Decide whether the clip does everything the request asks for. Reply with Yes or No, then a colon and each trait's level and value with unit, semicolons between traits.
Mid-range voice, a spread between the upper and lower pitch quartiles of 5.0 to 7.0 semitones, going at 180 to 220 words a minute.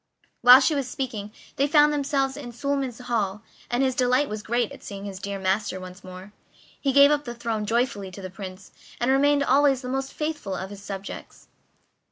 No: high, 245 Hz; wide, 5.4 semitones; average, 200 wpm